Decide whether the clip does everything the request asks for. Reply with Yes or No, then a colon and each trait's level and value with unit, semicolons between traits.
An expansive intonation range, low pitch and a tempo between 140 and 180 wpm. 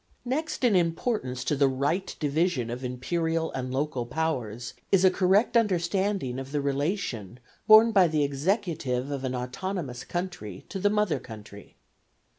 No: wide, 6.9 semitones; medium, 150 Hz; average, 150 wpm